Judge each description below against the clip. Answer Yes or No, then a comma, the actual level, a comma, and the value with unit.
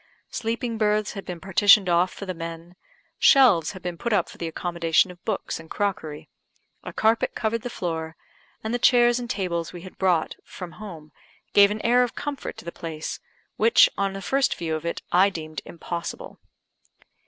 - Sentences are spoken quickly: No, average, 185 wpm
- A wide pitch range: No, average, 4.5 semitones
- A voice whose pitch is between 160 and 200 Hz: Yes, medium, 185 Hz